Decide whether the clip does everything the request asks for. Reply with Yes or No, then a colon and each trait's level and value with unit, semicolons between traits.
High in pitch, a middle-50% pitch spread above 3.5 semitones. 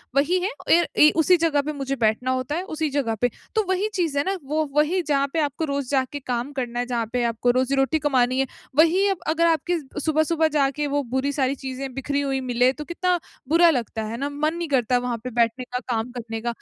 Yes: very high, 280 Hz; average, 4.0 semitones